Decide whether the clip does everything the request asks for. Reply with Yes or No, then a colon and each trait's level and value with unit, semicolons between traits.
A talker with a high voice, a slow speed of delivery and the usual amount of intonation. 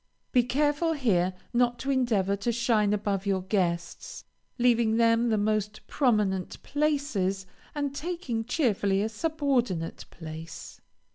Yes: high, 225 Hz; slow, 130 wpm; average, 4.9 semitones